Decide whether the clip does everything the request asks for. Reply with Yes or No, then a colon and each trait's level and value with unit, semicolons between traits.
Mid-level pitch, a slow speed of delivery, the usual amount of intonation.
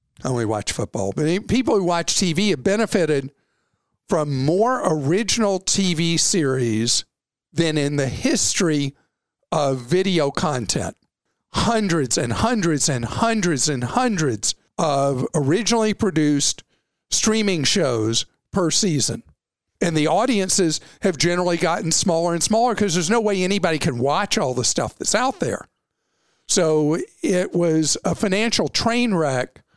No: medium, 170 Hz; slow, 130 wpm; wide, 5.8 semitones